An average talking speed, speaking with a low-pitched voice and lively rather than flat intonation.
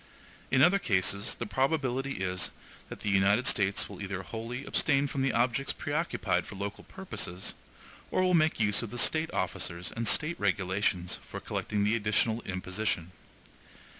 Yes: average, 160 wpm; low, 110 Hz; wide, 5.9 semitones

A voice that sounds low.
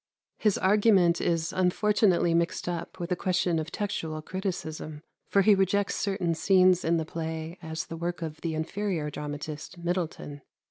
No: medium, 170 Hz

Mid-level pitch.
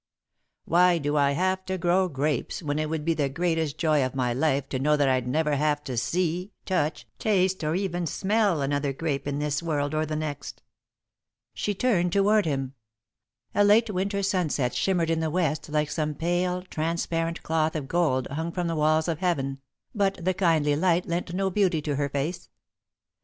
Yes: medium, 160 Hz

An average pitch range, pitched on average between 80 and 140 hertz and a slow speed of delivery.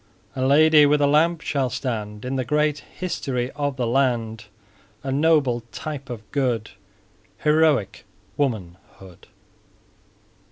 Yes: average, 4.1 semitones; low, 135 Hz; slow, 120 wpm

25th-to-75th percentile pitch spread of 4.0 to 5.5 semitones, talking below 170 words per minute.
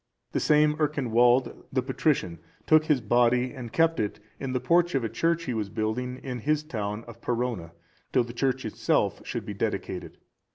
No: average, 4.4 semitones; average, 180 wpm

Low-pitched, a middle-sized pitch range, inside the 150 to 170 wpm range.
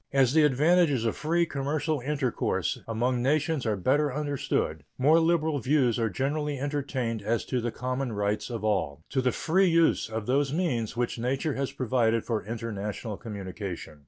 Yes: low, 130 Hz; average, 4.7 semitones; average, 165 wpm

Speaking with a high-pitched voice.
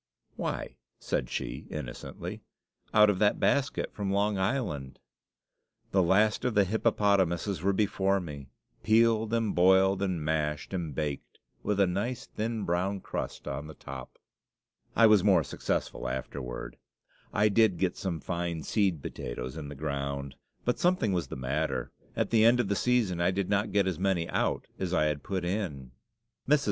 No: very low, 95 Hz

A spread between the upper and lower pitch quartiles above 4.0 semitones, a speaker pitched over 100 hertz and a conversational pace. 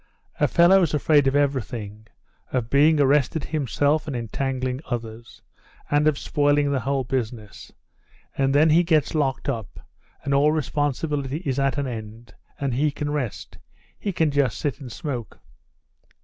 No: average, 3.0 semitones; medium, 140 Hz; average, 150 wpm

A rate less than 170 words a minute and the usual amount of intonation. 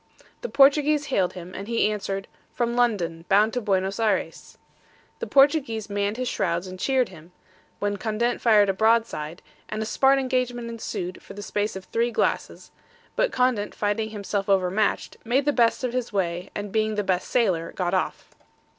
No: average, 180 wpm; average, 4.0 semitones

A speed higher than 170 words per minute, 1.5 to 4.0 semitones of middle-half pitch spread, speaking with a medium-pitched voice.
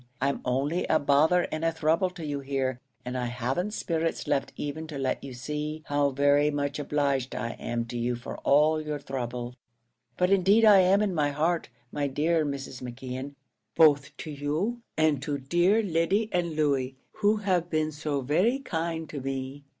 Yes: average, 180 wpm; average, 3.5 semitones; medium, 150 Hz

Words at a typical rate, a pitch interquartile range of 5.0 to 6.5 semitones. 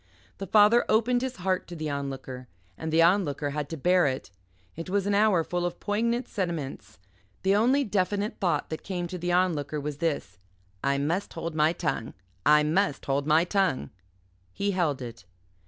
Yes: average, 180 wpm; average, 5.3 semitones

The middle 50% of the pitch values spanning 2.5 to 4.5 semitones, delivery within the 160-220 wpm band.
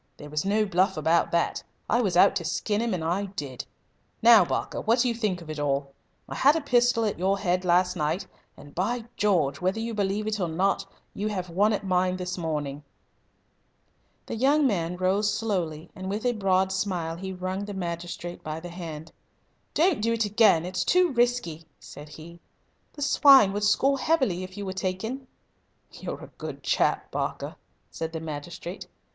Yes: average, 4.1 semitones; average, 190 wpm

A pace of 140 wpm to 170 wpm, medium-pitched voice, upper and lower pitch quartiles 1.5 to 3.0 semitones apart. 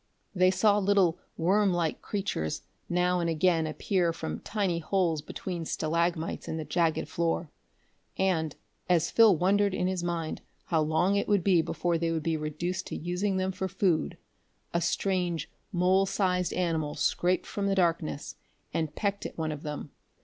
Yes: average, 165 wpm; medium, 175 Hz; narrow, 2.6 semitones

